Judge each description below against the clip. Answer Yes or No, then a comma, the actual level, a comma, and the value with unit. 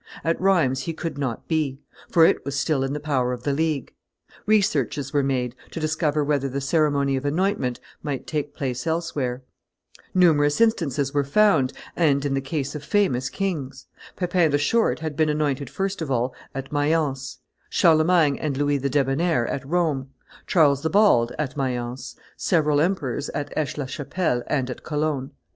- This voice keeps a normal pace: Yes, average, 170 wpm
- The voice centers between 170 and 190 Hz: No, medium, 145 Hz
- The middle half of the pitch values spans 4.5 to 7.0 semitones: No, average, 3.1 semitones